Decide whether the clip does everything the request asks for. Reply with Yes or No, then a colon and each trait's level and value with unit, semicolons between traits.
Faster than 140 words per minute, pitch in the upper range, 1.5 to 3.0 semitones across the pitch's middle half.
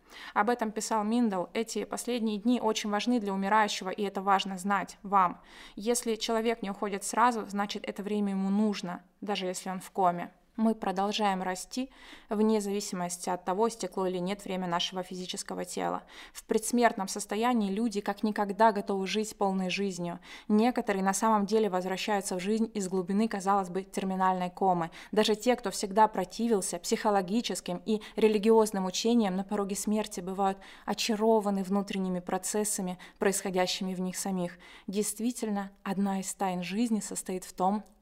Yes: average, 150 wpm; high, 200 Hz; narrow, 2.5 semitones